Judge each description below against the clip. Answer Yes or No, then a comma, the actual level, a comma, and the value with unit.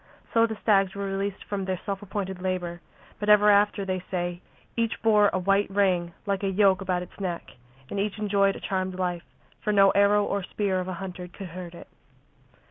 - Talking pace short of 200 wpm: No, fast, 205 wpm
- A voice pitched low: No, high, 195 Hz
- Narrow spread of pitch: Yes, narrow, 1.8 semitones